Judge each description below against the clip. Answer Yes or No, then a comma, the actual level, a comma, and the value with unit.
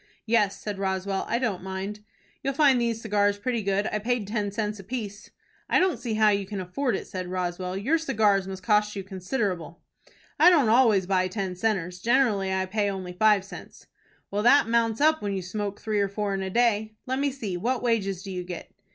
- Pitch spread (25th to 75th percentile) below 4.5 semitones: Yes, average, 3.3 semitones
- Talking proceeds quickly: Yes, fast, 210 wpm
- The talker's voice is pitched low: No, high, 205 Hz